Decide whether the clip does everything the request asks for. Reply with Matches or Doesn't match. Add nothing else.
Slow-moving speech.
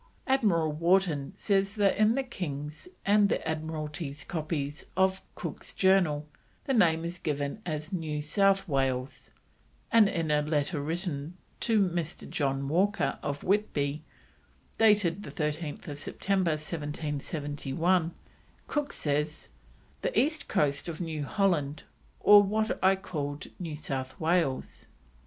Matches